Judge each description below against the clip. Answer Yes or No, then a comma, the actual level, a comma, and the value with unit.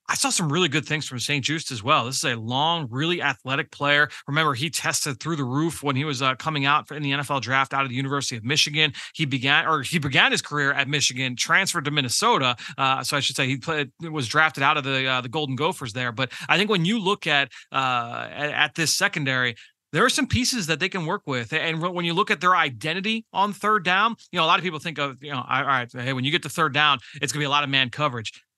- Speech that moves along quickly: Yes, fast, 265 wpm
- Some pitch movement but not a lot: Yes, average, 3.4 semitones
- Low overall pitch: No, medium, 150 Hz